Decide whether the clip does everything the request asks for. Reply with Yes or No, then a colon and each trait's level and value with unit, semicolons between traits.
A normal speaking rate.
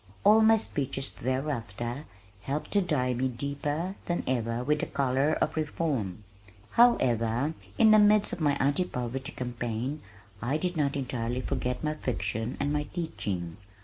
Yes: average, 150 wpm